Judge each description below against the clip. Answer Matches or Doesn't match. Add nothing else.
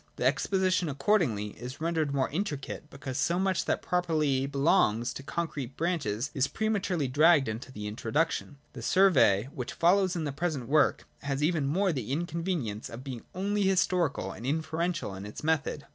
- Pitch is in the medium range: Matches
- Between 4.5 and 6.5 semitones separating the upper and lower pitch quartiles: Matches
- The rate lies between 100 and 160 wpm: Doesn't match